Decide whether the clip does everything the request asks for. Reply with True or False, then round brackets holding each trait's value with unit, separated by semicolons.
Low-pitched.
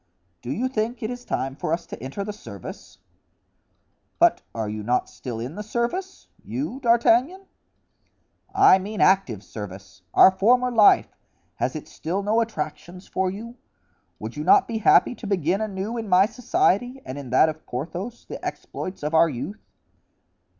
False (200 Hz)